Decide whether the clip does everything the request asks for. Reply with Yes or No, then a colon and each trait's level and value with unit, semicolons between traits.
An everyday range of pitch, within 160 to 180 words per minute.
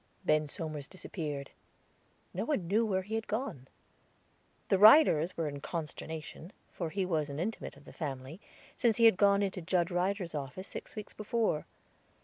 Yes: average, 5.0 semitones; average, 165 wpm